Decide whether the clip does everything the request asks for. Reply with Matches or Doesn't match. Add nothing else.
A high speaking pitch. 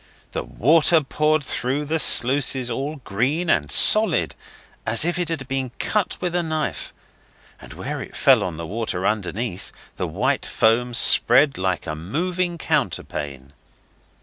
Doesn't match